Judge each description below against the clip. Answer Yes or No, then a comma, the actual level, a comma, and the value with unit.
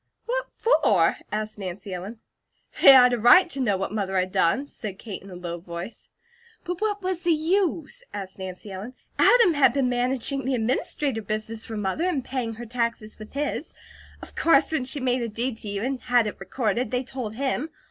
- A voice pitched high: Yes, high, 240 Hz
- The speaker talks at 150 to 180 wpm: No, average, 200 wpm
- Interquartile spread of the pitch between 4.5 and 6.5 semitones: Yes, average, 5.1 semitones